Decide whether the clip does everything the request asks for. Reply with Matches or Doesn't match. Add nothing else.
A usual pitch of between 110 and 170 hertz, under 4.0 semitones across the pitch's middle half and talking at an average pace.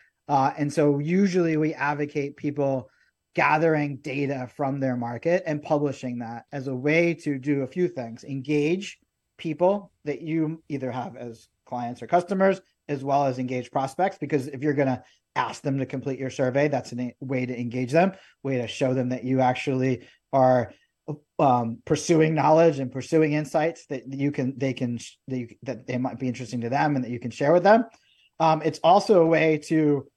Matches